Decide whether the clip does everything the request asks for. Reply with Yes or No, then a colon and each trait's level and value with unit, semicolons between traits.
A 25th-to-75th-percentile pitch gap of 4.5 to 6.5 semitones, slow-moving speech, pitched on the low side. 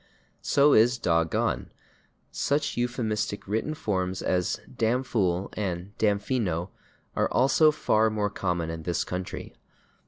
Yes: average, 5.0 semitones; slow, 120 wpm; low, 105 Hz